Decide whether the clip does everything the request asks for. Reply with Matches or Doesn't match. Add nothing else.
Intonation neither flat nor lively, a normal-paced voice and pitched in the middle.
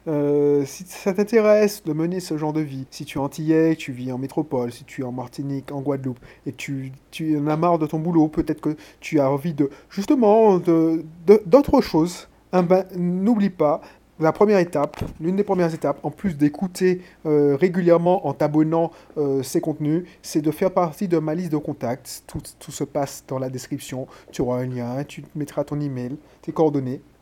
Matches